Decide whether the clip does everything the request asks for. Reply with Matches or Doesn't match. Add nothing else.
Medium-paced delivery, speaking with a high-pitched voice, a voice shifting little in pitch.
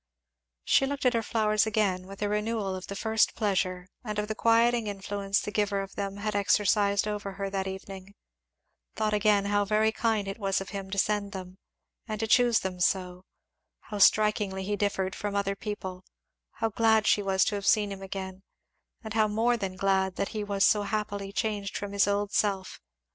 Matches